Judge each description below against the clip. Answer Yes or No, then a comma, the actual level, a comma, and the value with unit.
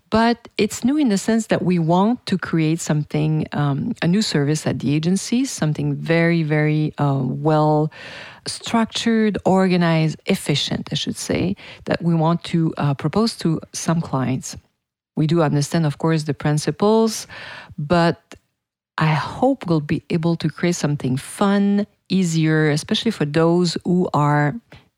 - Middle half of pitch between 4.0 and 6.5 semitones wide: Yes, average, 4.3 semitones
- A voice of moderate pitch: Yes, medium, 165 Hz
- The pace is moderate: Yes, average, 150 wpm